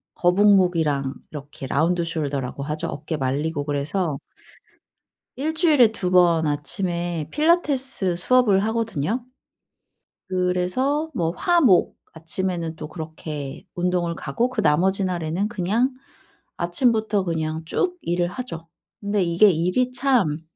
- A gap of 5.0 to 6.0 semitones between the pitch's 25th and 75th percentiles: Yes, wide, 5.6 semitones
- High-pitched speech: No, medium, 180 Hz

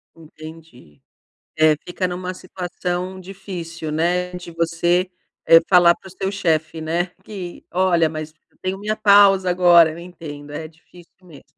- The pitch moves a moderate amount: No, narrow, 2.3 semitones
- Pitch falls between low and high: Yes, medium, 175 Hz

